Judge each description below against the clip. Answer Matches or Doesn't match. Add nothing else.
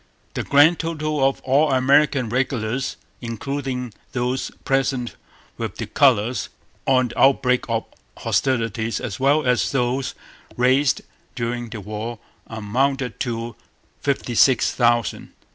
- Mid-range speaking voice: Doesn't match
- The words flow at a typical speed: Doesn't match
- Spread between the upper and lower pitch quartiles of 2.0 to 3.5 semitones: Matches